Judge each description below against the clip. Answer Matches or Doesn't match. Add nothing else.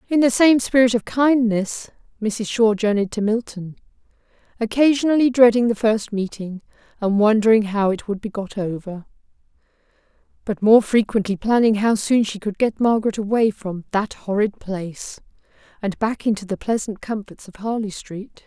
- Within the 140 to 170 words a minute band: Matches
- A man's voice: Doesn't match